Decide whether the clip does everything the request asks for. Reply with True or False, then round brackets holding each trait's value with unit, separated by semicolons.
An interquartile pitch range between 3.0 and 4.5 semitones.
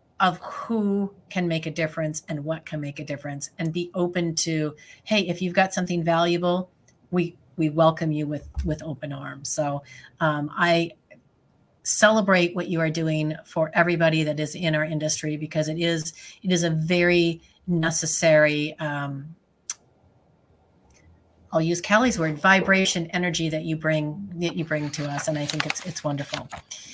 False (2.5 semitones)